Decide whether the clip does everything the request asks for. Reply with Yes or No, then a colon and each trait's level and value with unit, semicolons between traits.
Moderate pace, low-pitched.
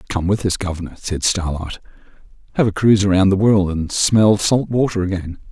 Yes: average, 185 wpm; very low, 95 Hz